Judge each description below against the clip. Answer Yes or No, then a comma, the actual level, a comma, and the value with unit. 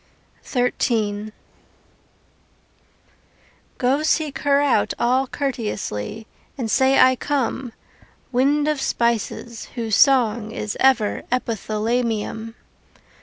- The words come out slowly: Yes, slow, 85 wpm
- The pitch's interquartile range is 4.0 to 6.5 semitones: No, average, 3.3 semitones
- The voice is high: Yes, high, 245 Hz